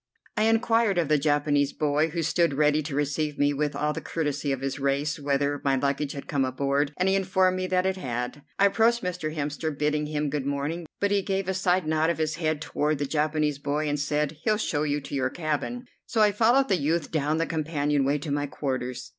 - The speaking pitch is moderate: Yes, medium, 150 Hz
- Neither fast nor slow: No, fast, 230 wpm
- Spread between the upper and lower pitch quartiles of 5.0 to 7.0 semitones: No, average, 3.4 semitones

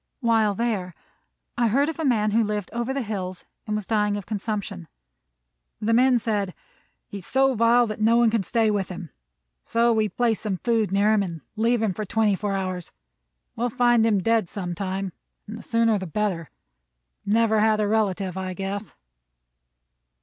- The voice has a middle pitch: No, high, 215 Hz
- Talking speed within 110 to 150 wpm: No, average, 185 wpm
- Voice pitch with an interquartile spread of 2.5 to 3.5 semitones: Yes, average, 2.8 semitones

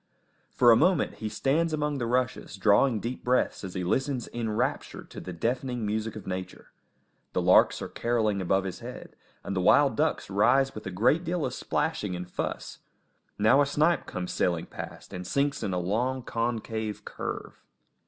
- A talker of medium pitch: No, low, 115 Hz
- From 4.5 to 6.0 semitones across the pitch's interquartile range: Yes, wide, 5.4 semitones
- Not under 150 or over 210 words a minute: Yes, average, 180 wpm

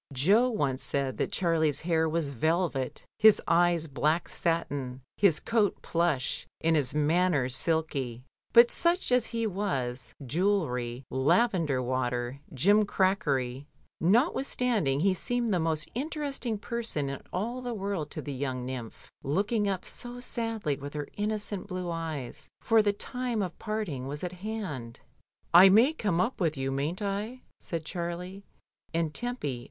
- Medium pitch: Yes, medium, 170 Hz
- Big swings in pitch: Yes, wide, 7.1 semitones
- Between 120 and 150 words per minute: Yes, average, 145 wpm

